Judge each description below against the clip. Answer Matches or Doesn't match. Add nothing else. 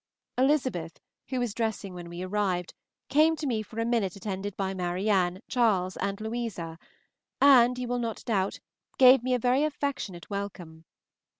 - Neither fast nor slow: Matches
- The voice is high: Matches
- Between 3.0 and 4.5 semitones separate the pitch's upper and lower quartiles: Doesn't match